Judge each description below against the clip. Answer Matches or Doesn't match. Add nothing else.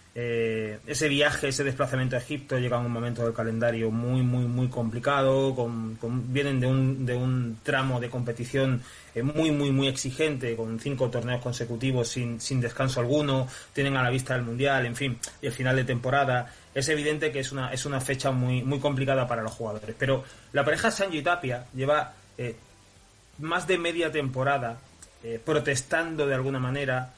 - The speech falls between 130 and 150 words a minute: Doesn't match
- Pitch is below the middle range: Matches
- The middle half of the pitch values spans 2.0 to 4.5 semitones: Matches